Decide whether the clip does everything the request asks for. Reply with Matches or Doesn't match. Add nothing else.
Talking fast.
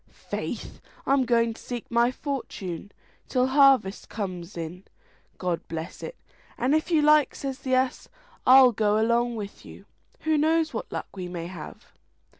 Doesn't match